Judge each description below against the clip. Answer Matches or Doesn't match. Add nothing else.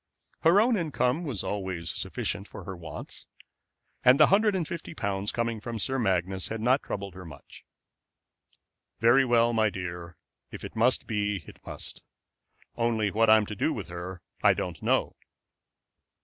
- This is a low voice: Matches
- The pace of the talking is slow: Doesn't match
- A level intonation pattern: Doesn't match